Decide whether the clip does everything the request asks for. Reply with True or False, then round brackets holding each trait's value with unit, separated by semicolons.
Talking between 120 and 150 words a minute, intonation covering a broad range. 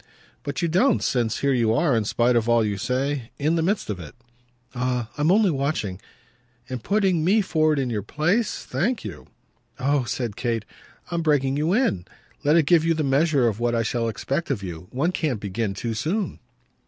False (205 wpm; 5.8 semitones)